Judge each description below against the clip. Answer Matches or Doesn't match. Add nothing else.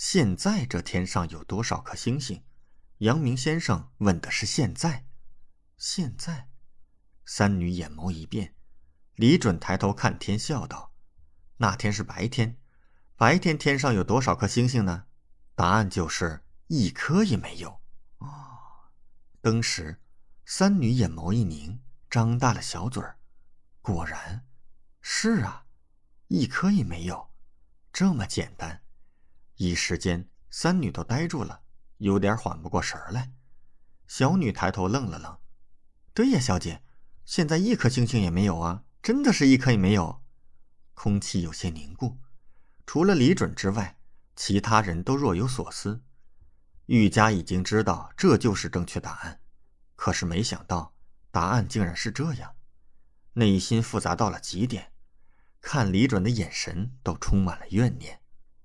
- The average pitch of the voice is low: Matches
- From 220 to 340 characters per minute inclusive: Doesn't match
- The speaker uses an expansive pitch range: Matches